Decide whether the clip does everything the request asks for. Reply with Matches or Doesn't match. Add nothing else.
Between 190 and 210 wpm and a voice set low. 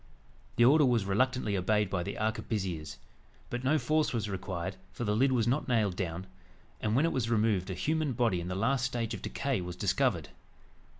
Matches